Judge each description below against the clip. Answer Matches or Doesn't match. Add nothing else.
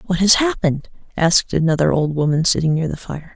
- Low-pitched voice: Doesn't match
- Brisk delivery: Doesn't match